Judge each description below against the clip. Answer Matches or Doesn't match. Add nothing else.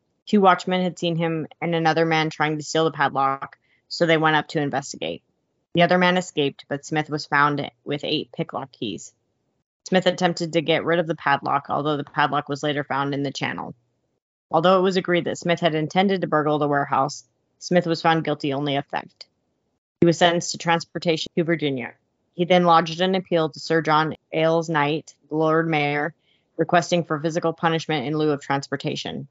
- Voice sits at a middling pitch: Matches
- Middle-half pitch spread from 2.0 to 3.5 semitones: Matches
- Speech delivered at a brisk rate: Doesn't match